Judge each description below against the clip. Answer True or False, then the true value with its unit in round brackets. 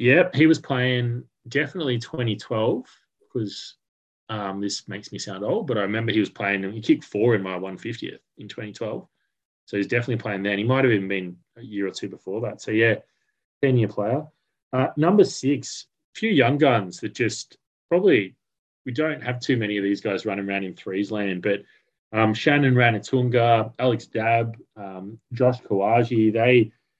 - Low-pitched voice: True (115 Hz)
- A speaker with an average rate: True (180 wpm)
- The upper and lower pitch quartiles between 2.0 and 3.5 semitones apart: False (3.9 semitones)